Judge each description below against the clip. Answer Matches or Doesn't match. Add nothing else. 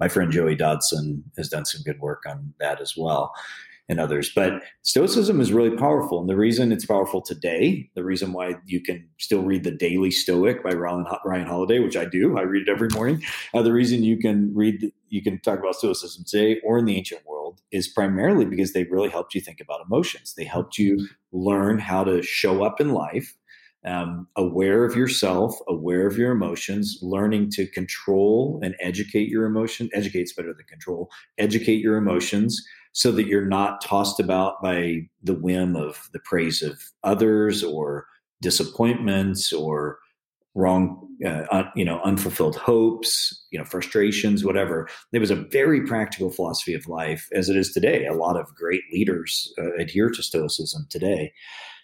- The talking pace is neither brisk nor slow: Matches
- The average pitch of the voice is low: Matches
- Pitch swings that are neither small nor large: Matches